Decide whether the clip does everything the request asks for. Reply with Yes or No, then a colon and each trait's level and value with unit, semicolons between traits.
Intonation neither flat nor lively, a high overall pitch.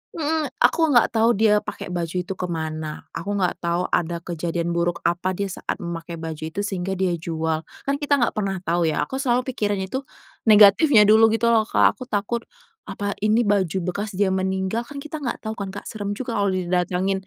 Yes: average, 4.3 semitones; high, 195 Hz